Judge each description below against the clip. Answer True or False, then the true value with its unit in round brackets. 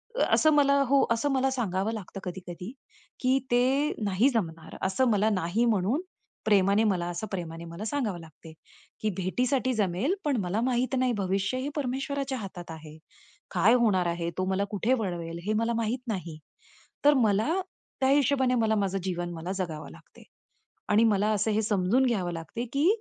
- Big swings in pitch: True (6.0 semitones)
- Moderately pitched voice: False (210 Hz)